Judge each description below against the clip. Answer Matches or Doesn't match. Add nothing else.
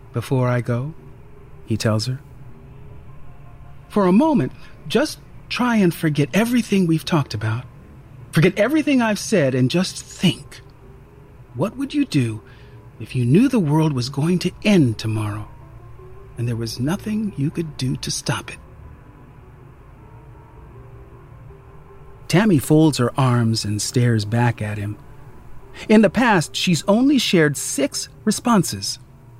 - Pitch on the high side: Doesn't match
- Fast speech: Doesn't match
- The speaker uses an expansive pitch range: Matches